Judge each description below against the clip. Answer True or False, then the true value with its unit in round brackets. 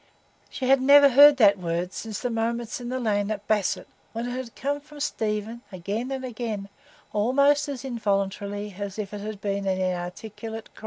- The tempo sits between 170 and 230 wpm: True (190 wpm)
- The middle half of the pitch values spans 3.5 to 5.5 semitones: True (4.2 semitones)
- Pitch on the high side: True (220 Hz)